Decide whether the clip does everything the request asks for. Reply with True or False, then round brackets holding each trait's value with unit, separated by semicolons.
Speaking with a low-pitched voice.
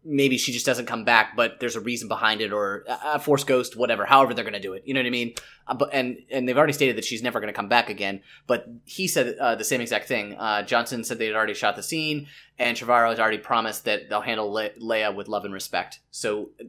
True (115 Hz)